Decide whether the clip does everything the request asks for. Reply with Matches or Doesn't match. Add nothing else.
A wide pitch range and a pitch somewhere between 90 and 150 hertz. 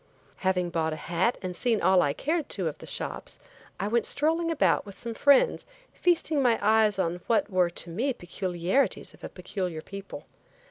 Doesn't match